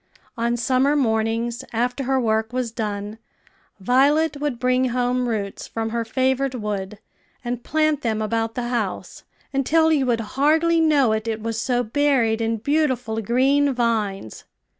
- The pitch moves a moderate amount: Yes, average, 3.3 semitones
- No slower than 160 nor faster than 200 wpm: No, average, 150 wpm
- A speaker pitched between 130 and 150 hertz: No, high, 240 Hz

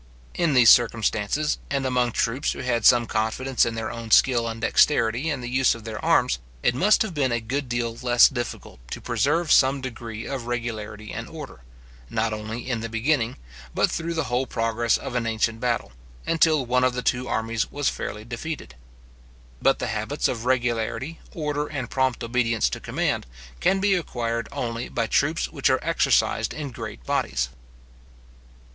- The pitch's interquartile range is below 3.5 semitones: Yes, average, 2.8 semitones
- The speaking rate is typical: Yes, average, 180 wpm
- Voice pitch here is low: Yes, low, 120 Hz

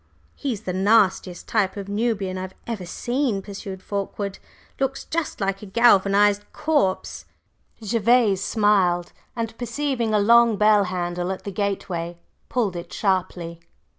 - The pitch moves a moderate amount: Yes, average, 3.4 semitones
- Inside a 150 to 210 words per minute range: No, slow, 135 wpm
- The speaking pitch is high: Yes, high, 200 Hz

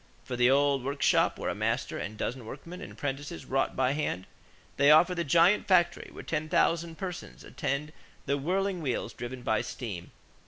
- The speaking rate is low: No, average, 185 wpm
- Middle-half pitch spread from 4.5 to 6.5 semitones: Yes, average, 4.8 semitones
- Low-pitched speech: No, medium, 145 Hz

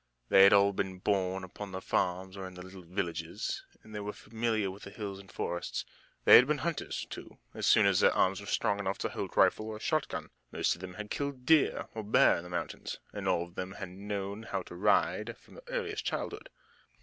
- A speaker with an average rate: No, fast, 225 wpm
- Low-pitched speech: Yes, low, 100 Hz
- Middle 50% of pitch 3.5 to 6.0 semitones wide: No, average, 2.8 semitones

